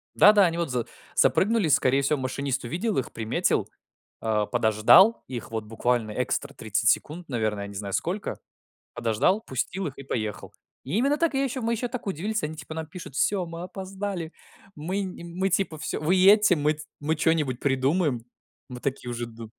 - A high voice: No, medium, 155 Hz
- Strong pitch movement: Yes, wide, 7.7 semitones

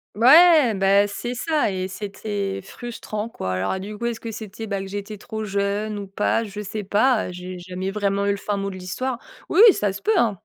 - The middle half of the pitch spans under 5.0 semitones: Yes, narrow, 2.4 semitones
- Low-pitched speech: No, high, 205 Hz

